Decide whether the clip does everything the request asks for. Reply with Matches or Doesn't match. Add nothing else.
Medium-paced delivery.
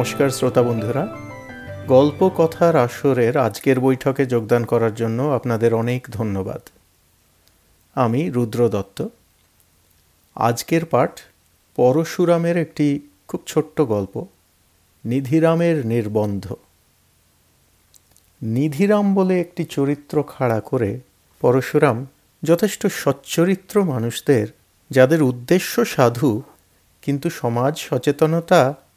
Matches